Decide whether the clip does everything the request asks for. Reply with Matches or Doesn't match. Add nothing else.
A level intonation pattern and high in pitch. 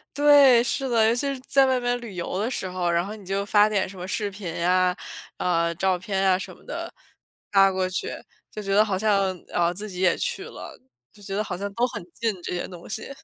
Doesn't match